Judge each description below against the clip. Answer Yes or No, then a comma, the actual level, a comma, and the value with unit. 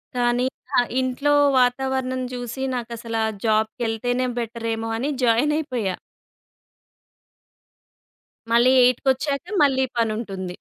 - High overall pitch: Yes, high, 245 Hz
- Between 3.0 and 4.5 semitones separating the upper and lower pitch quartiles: No, narrow, 2.5 semitones